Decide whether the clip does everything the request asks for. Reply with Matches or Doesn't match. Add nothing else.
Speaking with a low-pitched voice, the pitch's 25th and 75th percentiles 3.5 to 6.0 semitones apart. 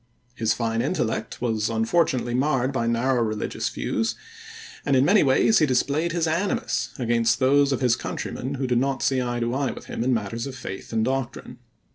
Doesn't match